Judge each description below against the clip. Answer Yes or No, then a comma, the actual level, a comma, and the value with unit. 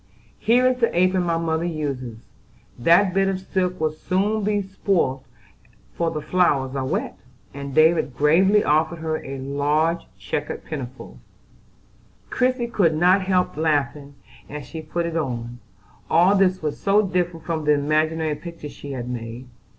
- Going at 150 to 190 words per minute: Yes, average, 155 wpm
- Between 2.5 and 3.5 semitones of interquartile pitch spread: No, average, 4.4 semitones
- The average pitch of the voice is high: No, medium, 160 Hz